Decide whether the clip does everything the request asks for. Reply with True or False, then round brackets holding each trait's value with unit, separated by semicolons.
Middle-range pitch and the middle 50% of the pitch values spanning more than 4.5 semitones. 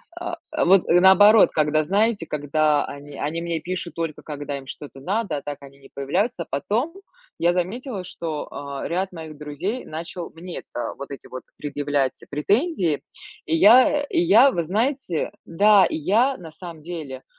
True (170 Hz; 5.6 semitones)